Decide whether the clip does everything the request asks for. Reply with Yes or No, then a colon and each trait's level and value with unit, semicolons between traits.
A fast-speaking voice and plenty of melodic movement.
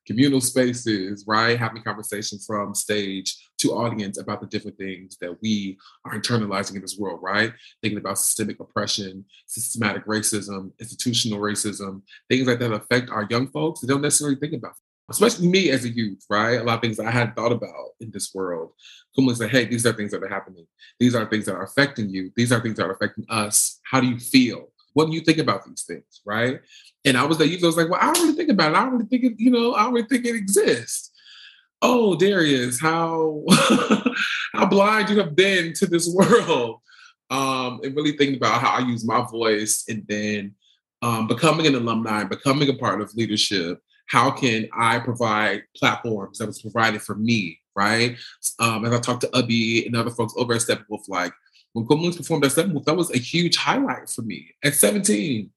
Yes: fast, 210 wpm; wide, 6.2 semitones